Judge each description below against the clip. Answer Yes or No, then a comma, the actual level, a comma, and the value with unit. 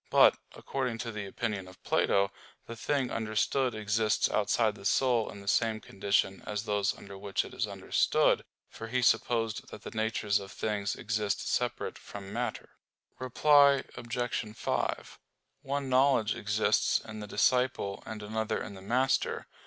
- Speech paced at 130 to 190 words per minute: Yes, average, 155 wpm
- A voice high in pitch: No, low, 110 Hz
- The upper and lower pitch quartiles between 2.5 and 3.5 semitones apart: Yes, average, 3.0 semitones